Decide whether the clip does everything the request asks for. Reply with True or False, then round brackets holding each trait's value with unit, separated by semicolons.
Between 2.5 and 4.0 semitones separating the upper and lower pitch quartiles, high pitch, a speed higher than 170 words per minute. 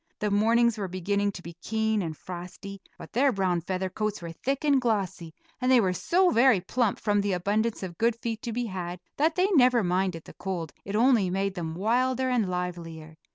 False (4.7 semitones; 200 Hz; 205 wpm)